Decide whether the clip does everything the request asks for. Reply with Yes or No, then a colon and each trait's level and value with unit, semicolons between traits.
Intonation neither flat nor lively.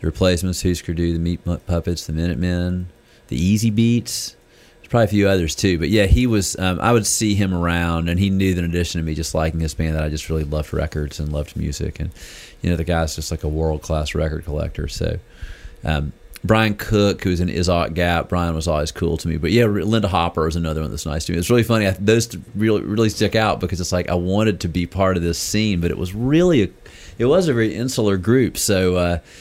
Yes: average, 4.0 semitones